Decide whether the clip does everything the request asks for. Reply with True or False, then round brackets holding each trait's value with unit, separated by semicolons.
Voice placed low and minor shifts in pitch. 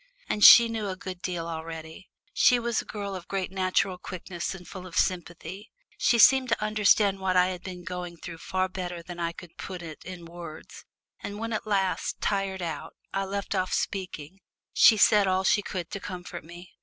False (185 Hz; 2.3 semitones)